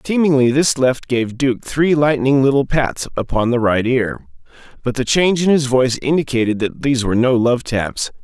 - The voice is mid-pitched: No, low, 130 Hz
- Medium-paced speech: Yes, average, 190 wpm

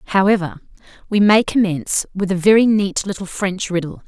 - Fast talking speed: No, average, 160 wpm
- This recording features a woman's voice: Yes, female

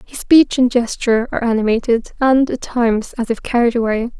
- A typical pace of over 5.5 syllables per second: Yes, 5.7 syllables/s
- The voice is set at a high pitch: Yes, high, 240 Hz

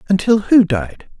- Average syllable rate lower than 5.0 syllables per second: Yes, 4.4 syllables/s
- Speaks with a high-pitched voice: No, medium, 180 Hz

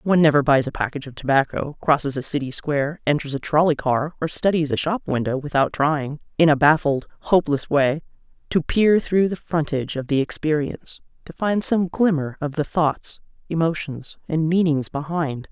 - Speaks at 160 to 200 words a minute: Yes, average, 180 wpm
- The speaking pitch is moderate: Yes, medium, 150 Hz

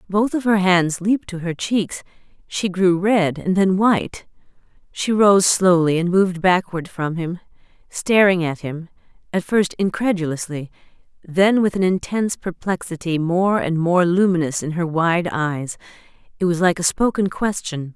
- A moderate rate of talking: Yes, average, 155 wpm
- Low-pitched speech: No, medium, 180 Hz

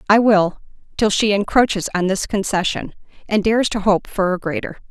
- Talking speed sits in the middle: Yes, average, 185 wpm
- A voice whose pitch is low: No, high, 200 Hz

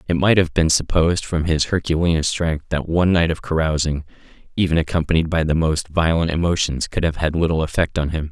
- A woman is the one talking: No, male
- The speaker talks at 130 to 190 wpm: No, average, 200 wpm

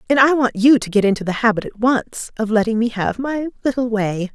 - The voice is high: Yes, high, 230 Hz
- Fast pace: Yes, fast, 250 wpm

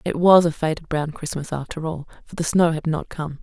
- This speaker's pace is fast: Yes, fast, 245 wpm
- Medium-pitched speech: Yes, medium, 160 Hz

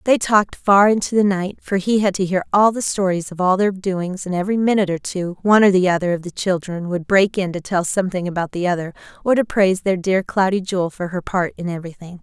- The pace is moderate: No, fast, 250 wpm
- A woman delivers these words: Yes, female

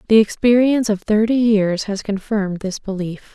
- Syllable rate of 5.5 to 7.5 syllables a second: No, 5.1 syllables/s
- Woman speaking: Yes, female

